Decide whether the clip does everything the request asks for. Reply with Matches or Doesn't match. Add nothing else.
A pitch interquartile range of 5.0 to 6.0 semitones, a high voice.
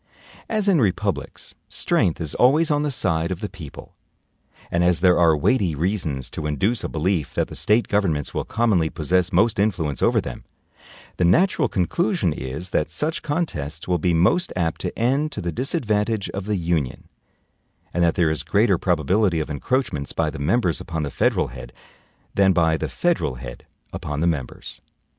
Doesn't match